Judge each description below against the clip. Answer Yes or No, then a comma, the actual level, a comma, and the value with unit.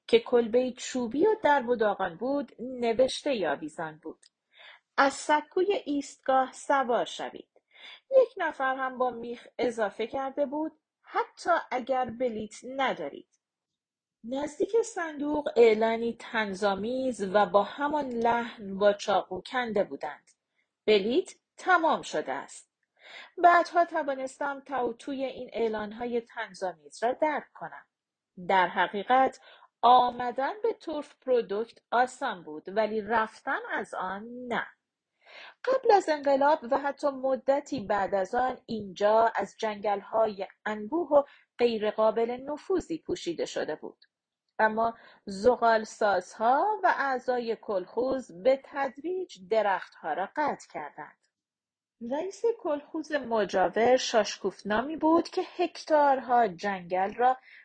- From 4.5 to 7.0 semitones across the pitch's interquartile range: Yes, average, 5.1 semitones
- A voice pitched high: Yes, very high, 250 Hz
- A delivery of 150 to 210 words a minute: No, average, 110 wpm